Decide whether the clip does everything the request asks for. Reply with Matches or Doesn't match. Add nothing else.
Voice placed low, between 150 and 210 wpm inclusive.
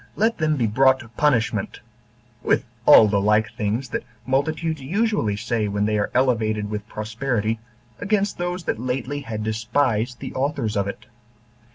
Matches